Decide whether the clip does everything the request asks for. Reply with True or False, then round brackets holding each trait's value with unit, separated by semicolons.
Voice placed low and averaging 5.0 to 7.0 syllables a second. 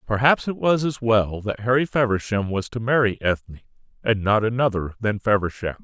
True (110 Hz; 5.3 syllables/s)